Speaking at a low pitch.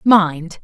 No: medium, 180 Hz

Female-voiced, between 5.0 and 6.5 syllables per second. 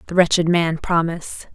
Yes: female; 5.3 syllables/s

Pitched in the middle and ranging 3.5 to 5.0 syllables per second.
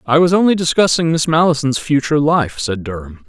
No: medium, 150 Hz; 5.7 syllables/s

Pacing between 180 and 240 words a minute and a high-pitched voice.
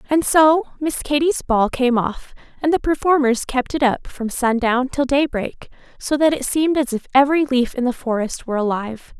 Yes: average, 195 wpm; very high, 265 Hz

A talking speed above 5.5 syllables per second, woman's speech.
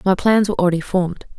Yes: 7.6 syllables/s; female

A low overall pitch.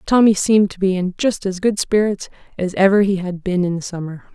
No: high, 190 Hz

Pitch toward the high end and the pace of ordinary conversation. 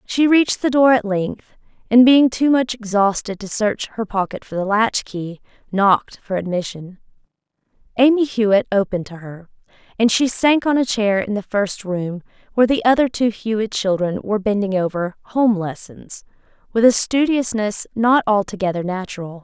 Yes: high, 215 Hz; average, 165 wpm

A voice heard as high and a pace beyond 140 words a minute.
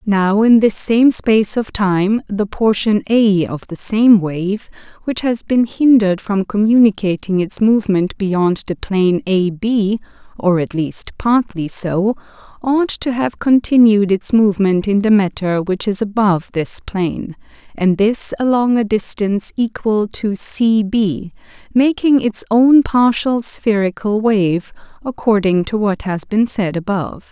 Yes: high, 210 Hz; average, 150 wpm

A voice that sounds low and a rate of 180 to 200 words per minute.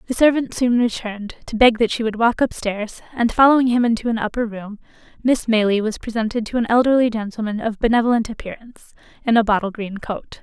No: high, 225 Hz; average, 195 wpm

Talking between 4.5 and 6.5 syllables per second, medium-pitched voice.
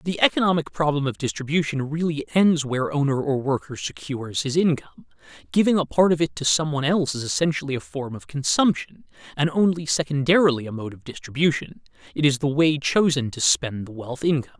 Yes: 6.0 syllables/s; medium, 145 Hz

